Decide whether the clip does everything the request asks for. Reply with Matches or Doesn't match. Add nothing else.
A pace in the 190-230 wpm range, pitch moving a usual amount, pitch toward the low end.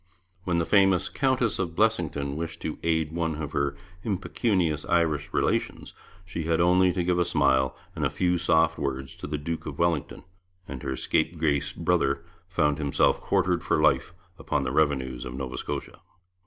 Doesn't match